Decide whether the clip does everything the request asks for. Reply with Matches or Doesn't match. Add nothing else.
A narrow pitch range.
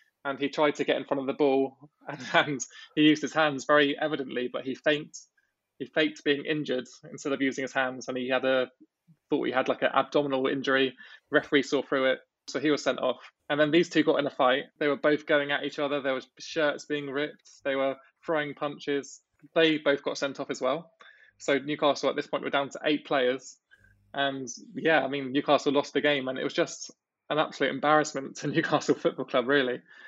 Matches